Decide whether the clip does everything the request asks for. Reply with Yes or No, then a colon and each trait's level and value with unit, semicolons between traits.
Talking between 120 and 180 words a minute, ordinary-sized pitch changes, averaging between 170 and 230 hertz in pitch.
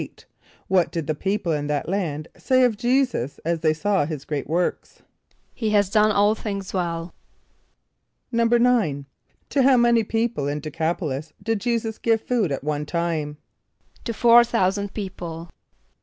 No: average, 160 wpm; wide, 6.5 semitones; high, 190 Hz